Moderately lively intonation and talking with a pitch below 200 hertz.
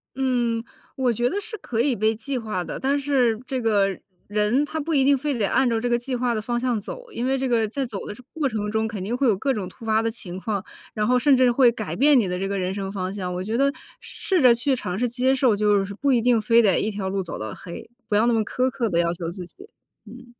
No: average, 4.1 semitones; high, 230 Hz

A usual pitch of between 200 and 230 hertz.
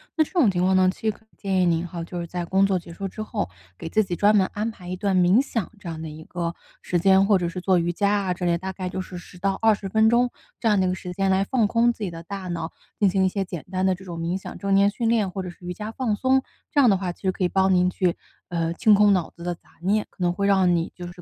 No: high, 190 Hz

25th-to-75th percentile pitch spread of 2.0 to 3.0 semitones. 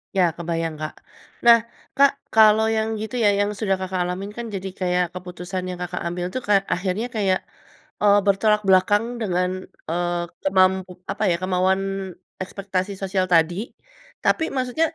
Yes: narrow, 2.5 semitones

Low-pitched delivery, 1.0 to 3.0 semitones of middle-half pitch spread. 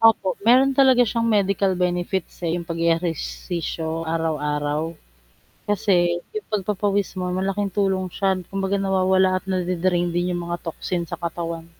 No: medium, 185 Hz; narrow, 2.6 semitones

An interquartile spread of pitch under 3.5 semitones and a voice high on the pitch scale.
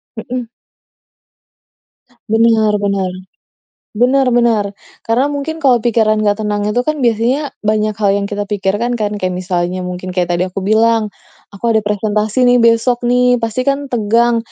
Yes: average, 2.9 semitones; high, 220 Hz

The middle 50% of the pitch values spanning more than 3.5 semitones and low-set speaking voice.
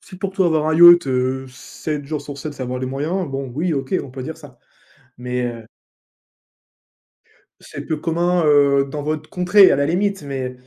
No: average, 4.4 semitones; medium, 150 Hz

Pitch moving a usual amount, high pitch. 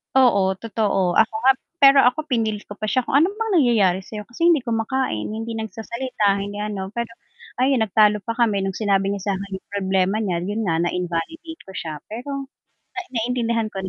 Yes: average, 3.9 semitones; high, 215 Hz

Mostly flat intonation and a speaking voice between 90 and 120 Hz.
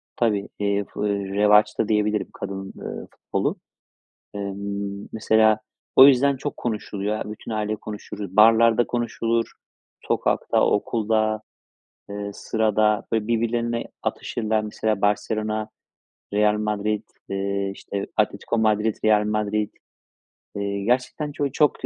Yes: narrow, 1.6 semitones; low, 105 Hz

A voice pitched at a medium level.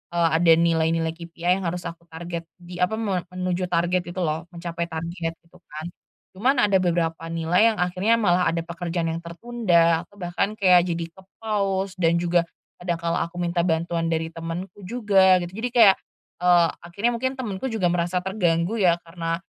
Yes: medium, 175 Hz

